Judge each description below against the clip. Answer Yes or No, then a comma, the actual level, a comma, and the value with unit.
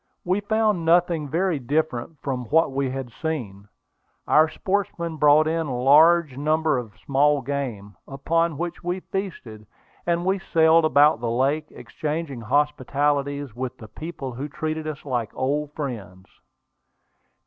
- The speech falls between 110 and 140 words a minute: Yes, slow, 135 wpm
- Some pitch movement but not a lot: Yes, average, 3.9 semitones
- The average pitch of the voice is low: No, medium, 150 Hz